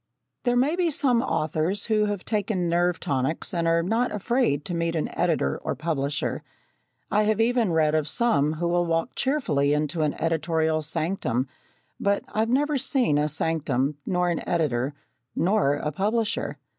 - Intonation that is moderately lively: No, wide, 6.1 semitones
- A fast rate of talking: No, average, 165 wpm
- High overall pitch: No, medium, 170 Hz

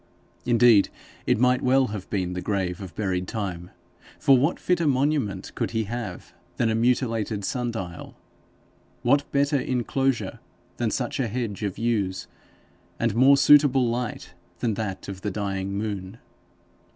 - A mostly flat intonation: No, average, 4.5 semitones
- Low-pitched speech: Yes, low, 115 Hz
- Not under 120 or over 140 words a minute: No, average, 150 wpm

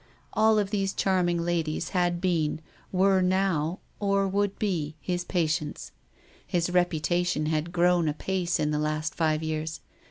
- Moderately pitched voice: Yes, medium, 175 Hz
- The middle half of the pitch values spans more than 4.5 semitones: No, average, 3.3 semitones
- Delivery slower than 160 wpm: Yes, average, 150 wpm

